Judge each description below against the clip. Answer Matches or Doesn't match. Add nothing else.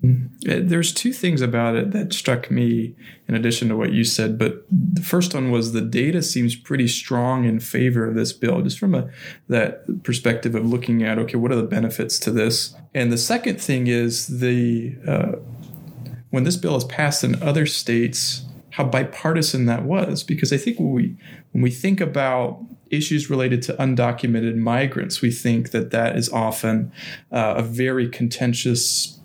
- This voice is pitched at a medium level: Doesn't match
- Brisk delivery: Doesn't match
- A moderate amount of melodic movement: Matches